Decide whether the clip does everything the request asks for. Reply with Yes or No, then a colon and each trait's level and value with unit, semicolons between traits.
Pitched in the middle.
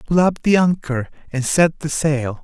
Yes: medium, 150 Hz